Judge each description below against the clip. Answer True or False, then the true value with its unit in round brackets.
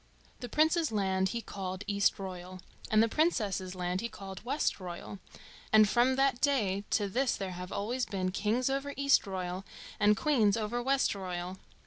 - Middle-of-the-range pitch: False (205 Hz)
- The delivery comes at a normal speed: True (150 wpm)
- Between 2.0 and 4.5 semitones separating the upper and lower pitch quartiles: False (4.9 semitones)